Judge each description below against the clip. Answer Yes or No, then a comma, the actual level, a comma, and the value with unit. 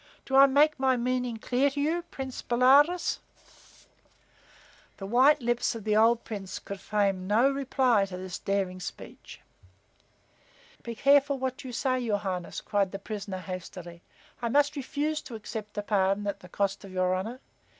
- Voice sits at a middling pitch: No, high, 230 Hz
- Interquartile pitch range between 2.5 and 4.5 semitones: No, average, 5.3 semitones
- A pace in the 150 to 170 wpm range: Yes, average, 165 wpm